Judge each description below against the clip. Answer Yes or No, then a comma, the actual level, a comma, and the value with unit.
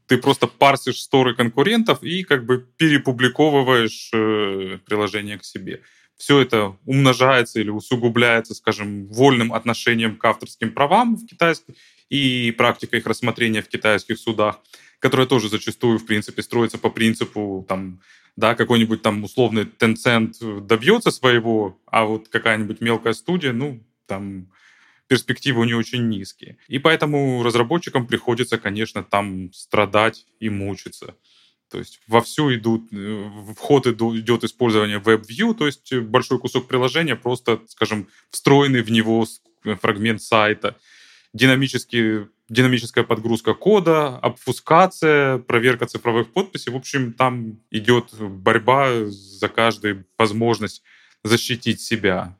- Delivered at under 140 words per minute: Yes, average, 125 wpm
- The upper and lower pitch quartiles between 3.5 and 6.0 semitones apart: No, average, 2.8 semitones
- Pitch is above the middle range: No, low, 115 Hz